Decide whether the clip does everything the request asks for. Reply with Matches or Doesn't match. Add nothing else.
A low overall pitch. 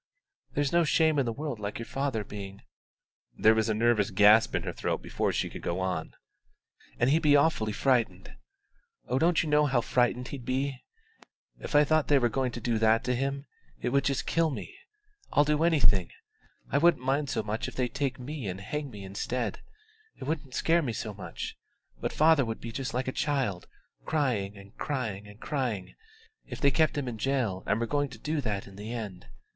Matches